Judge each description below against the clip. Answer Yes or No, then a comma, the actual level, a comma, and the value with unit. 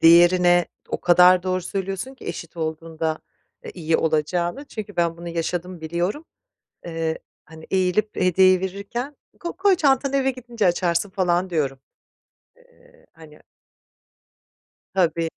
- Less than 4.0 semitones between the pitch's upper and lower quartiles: Yes, average, 3.6 semitones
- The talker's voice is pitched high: No, medium, 180 Hz